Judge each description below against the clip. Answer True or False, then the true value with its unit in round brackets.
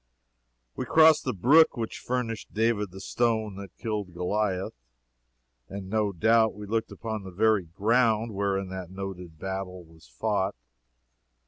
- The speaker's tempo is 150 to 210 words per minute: False (140 wpm)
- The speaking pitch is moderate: False (105 Hz)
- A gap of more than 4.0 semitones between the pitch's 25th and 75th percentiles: False (3.1 semitones)